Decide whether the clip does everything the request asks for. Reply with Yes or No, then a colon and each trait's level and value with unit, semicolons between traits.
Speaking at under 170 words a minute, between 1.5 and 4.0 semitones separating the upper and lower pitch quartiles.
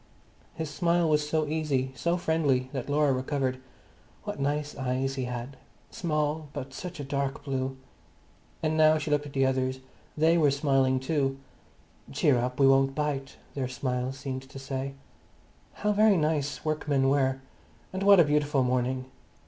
Yes: average, 160 wpm; narrow, 2.5 semitones